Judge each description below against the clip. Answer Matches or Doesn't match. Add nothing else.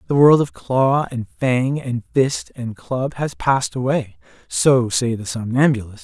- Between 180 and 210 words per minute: Doesn't match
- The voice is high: Doesn't match